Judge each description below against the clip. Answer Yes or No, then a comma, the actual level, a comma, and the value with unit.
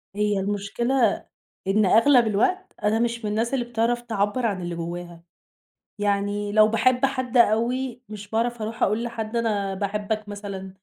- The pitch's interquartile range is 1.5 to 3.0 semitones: Yes, average, 2.7 semitones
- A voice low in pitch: No, high, 215 Hz